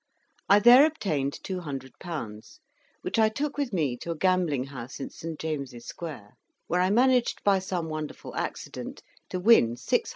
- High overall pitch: No, medium, 170 Hz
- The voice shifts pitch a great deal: Yes, wide, 6.7 semitones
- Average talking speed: Yes, average, 160 wpm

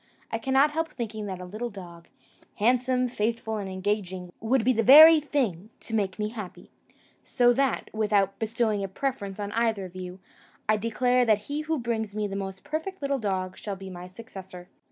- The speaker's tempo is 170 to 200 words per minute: Yes, average, 190 wpm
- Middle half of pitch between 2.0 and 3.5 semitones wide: No, average, 4.4 semitones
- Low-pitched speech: No, high, 215 Hz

